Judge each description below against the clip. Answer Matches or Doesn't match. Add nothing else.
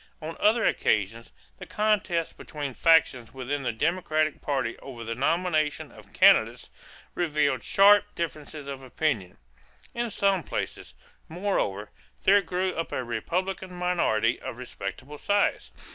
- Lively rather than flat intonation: Matches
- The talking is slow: Matches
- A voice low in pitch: Doesn't match